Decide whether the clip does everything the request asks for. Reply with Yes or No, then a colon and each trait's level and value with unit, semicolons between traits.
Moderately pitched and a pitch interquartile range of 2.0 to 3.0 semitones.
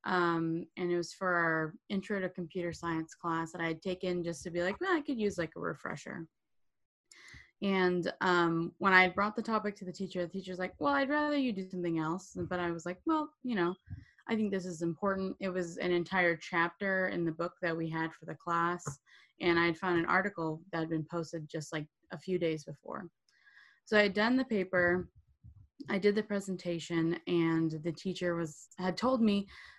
Yes: medium, 175 Hz; narrow, 2.5 semitones